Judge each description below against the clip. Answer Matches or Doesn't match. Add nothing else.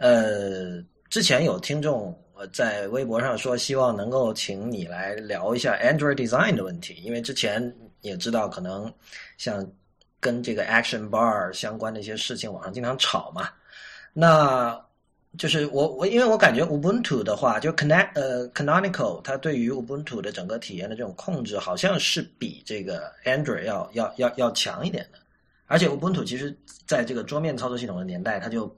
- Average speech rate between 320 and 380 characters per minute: Matches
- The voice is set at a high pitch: Doesn't match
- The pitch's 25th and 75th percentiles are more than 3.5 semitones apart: Matches